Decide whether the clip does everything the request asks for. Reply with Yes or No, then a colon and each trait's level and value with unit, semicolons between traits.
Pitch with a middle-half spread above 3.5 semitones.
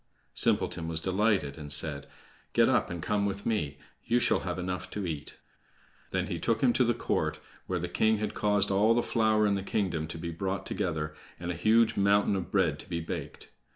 Yes: average, 4.1 semitones